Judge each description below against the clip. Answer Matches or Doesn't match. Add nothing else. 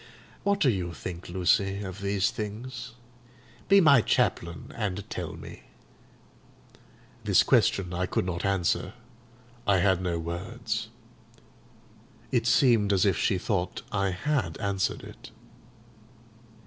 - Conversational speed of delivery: Doesn't match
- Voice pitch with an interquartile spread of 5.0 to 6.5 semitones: Doesn't match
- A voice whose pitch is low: Matches